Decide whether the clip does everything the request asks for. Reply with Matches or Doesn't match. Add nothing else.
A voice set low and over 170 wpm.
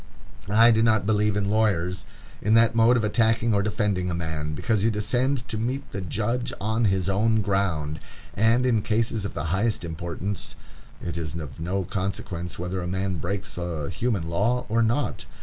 Matches